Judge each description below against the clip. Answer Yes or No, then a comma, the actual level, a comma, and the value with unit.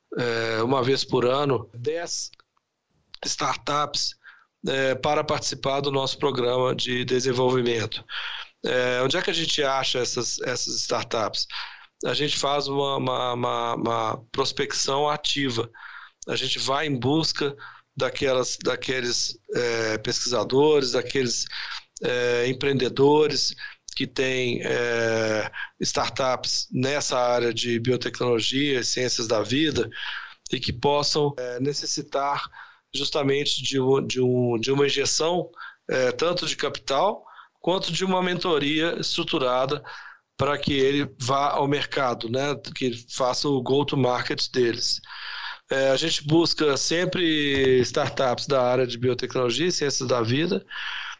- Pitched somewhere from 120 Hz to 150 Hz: Yes, low, 135 Hz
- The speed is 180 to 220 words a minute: No, average, 125 wpm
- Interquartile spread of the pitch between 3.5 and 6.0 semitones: No, average, 2.8 semitones